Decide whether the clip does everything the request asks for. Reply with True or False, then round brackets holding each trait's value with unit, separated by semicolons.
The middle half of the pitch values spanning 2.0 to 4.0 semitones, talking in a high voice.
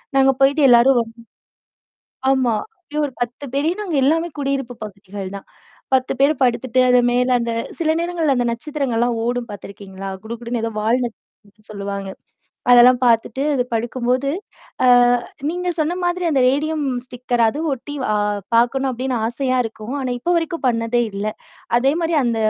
True (3.3 semitones; 250 Hz)